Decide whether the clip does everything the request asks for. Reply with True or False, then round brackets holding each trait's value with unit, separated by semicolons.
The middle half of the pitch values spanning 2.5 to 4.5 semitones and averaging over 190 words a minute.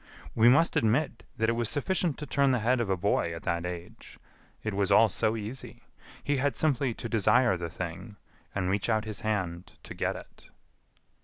False (4.9 semitones; 200 wpm)